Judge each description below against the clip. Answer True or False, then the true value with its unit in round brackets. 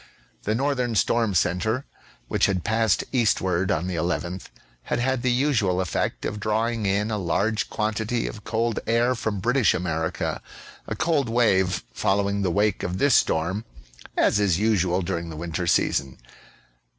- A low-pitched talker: True (105 Hz)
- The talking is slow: False (155 wpm)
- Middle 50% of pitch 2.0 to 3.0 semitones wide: False (4.1 semitones)